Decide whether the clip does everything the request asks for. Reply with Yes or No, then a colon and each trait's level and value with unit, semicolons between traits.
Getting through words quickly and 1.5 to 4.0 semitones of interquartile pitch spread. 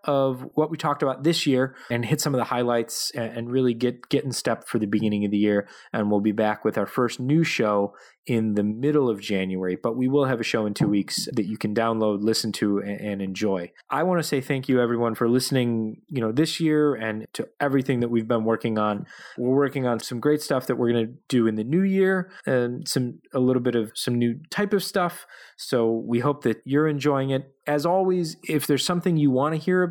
No: fast, 240 wpm; average, 4.5 semitones